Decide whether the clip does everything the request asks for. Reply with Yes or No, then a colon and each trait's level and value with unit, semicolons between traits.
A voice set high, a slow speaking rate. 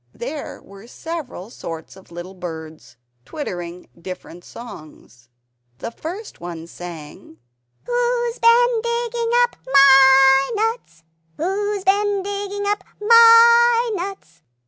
Yes: very high, 320 Hz; slow, 105 wpm